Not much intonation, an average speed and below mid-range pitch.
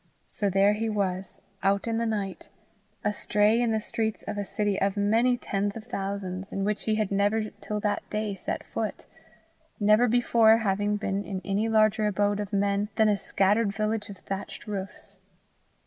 No: narrow, 1.6 semitones; average, 180 wpm; high, 205 Hz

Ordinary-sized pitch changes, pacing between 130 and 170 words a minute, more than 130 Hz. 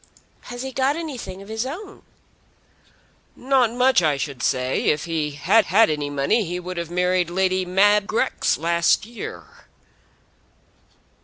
No: wide, 6.3 semitones; average, 145 wpm; medium, 185 Hz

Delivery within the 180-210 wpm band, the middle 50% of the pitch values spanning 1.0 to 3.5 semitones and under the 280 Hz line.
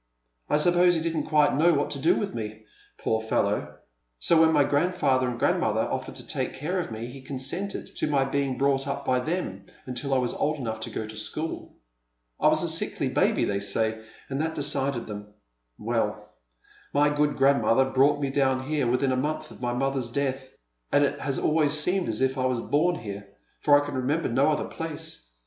Yes: fast, 205 wpm; average, 3.2 semitones; low, 135 Hz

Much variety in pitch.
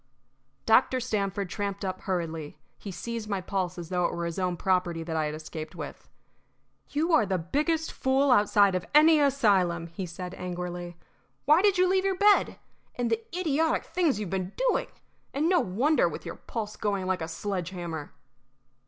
Yes: wide, 7.5 semitones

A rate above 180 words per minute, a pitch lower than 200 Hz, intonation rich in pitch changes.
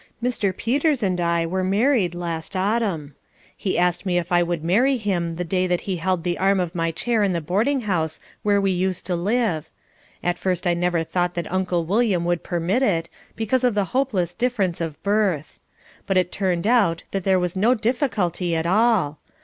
No: average, 200 wpm; medium, 185 Hz; average, 3.6 semitones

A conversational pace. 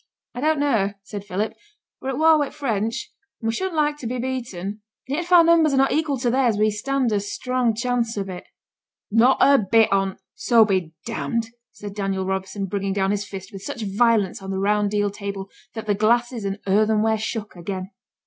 No: fast, 215 wpm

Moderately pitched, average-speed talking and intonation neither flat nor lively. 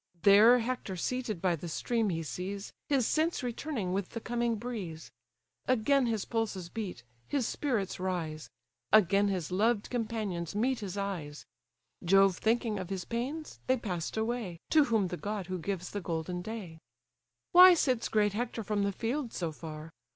No: high, 205 Hz; average, 165 wpm; average, 4.7 semitones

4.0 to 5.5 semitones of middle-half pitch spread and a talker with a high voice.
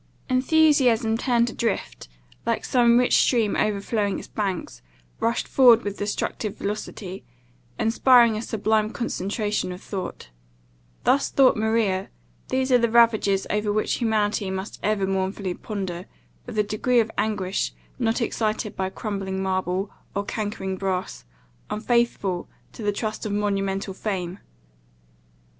No: average, 3.0 semitones; high, 210 Hz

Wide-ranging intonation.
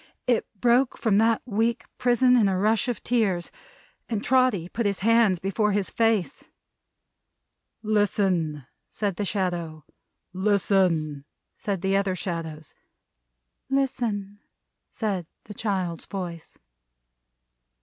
No: average, 3.9 semitones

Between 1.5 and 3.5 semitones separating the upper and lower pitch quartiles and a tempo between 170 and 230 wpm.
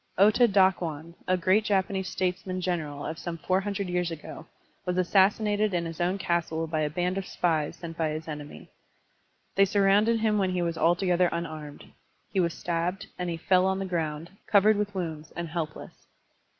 Yes: average, 2.8 semitones; average, 180 wpm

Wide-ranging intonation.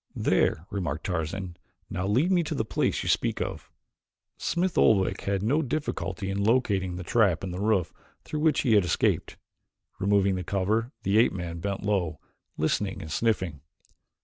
No: average, 3.8 semitones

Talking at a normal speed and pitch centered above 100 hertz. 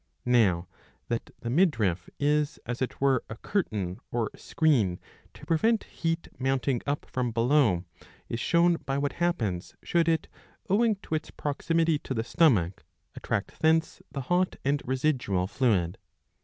Yes: average, 145 wpm; low, 135 Hz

